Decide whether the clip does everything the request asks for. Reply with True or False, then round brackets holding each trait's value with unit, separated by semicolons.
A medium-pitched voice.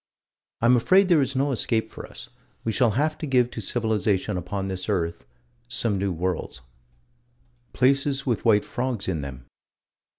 False (115 Hz)